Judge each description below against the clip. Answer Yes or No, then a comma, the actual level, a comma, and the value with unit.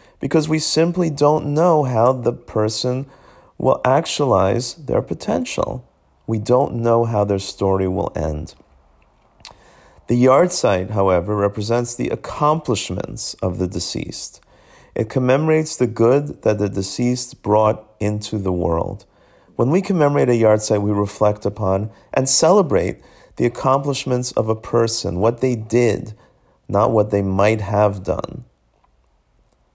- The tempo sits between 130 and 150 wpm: Yes, slow, 135 wpm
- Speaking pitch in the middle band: No, low, 110 Hz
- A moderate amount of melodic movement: Yes, average, 4.5 semitones